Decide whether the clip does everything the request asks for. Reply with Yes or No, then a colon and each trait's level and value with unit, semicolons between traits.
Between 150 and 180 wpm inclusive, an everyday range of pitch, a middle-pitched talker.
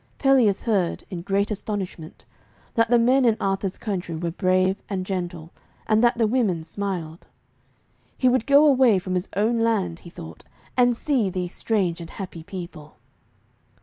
No: average, 160 wpm; average, 4.5 semitones; high, 195 Hz